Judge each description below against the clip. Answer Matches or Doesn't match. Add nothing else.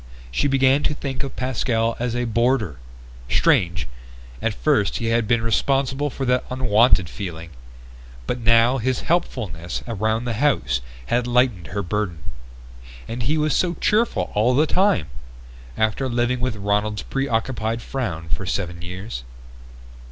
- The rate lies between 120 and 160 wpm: Matches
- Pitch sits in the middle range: Doesn't match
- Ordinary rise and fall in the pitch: Matches